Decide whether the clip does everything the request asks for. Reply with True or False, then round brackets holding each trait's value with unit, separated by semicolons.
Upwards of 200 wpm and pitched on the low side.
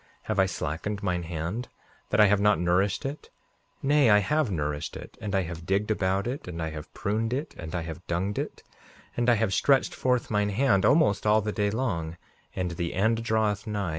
True (210 wpm; 100 Hz)